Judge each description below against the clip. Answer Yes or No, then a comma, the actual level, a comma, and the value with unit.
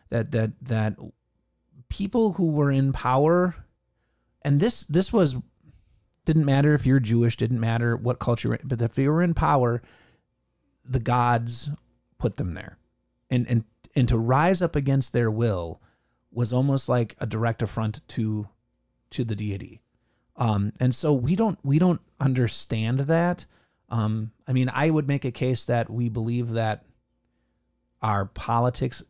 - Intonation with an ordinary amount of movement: Yes, average, 4.0 semitones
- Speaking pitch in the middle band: No, low, 120 Hz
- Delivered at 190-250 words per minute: No, average, 155 wpm